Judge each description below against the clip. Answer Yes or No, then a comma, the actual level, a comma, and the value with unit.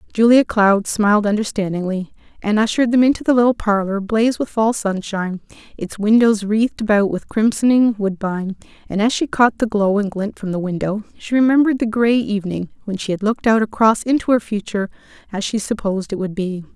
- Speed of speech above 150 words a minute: Yes, average, 190 wpm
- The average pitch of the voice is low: No, high, 210 Hz